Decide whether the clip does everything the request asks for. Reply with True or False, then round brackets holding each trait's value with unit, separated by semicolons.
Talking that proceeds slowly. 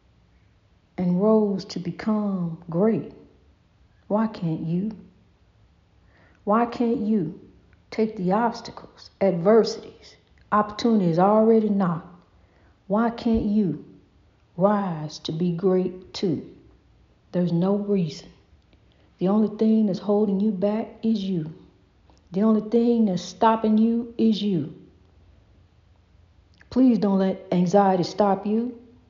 True (105 wpm)